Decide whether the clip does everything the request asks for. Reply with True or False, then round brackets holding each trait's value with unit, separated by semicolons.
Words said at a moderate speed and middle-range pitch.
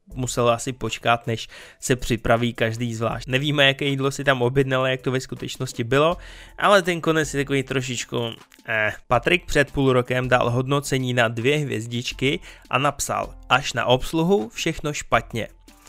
False (160 wpm; 130 Hz)